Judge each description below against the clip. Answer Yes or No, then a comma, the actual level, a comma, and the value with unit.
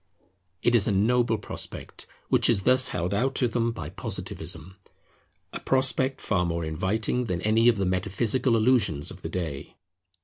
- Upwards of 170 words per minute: No, average, 165 wpm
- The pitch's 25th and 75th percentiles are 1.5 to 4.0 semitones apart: No, average, 4.9 semitones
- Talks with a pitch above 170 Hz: No, low, 105 Hz